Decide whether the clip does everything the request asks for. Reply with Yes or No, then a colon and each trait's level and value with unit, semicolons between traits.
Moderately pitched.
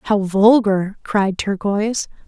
No: high, 205 Hz